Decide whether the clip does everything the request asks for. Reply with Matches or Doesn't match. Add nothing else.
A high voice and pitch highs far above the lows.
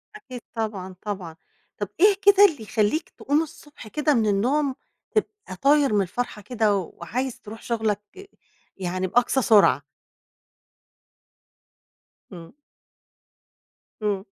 Matches